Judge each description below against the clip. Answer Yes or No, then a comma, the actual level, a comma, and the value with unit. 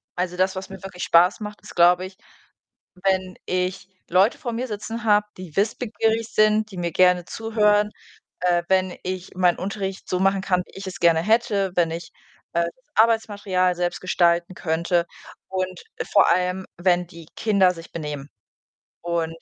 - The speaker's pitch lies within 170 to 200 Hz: Yes, medium, 185 Hz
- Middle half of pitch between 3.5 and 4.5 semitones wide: No, average, 2.8 semitones